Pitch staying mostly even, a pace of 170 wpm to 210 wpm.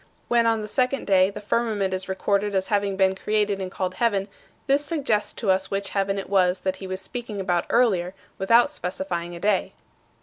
Yes: narrow, 2.3 semitones; average, 200 wpm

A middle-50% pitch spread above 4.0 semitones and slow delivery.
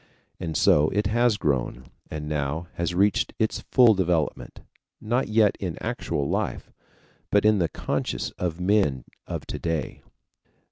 No: wide, 5.4 semitones; average, 145 wpm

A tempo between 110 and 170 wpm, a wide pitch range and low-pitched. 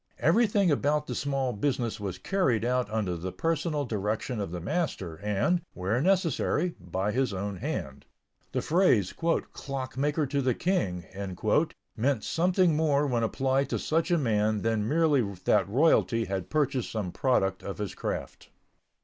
Yes: average, 150 wpm; wide, 6.7 semitones; low, 130 Hz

